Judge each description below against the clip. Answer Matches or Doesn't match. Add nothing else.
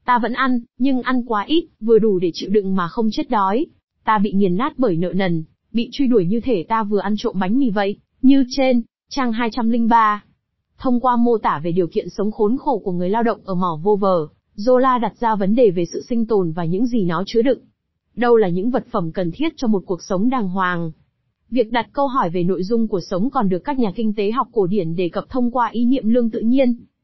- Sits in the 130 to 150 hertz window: Doesn't match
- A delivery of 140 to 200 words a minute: Doesn't match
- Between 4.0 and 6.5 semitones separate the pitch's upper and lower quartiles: Matches